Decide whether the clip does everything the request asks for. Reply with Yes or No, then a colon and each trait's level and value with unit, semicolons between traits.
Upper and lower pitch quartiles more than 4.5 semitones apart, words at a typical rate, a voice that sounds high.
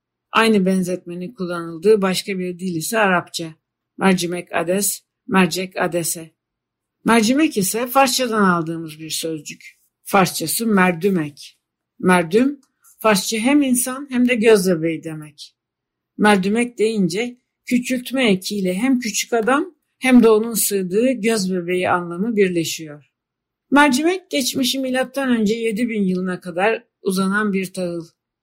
Yes: average, 5.1 semitones; average, 115 wpm; high, 200 Hz